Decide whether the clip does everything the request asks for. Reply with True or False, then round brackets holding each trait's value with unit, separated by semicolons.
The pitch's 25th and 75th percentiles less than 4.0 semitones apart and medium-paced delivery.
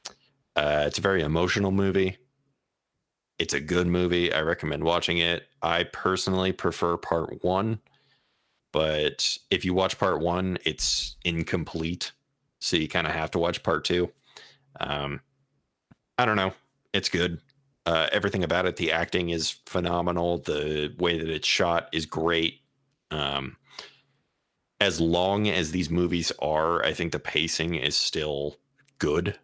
True (2.8 semitones; 145 wpm)